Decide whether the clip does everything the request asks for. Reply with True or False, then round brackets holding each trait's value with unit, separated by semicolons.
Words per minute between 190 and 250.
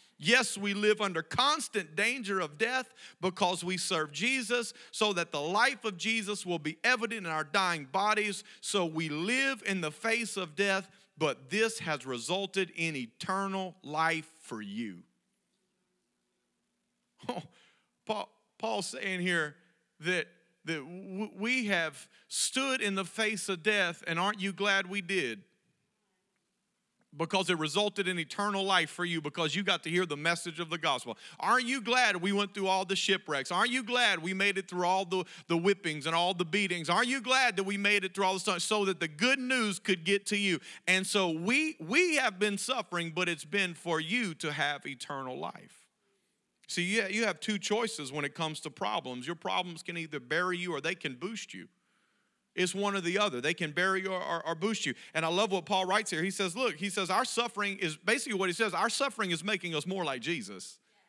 True (200 wpm)